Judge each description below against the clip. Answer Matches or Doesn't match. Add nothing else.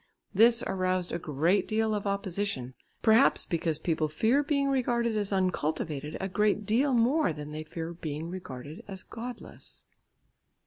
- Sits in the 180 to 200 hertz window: Matches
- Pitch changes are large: Matches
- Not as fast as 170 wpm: Matches